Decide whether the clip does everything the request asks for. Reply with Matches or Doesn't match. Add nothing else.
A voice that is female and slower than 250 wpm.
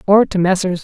Matches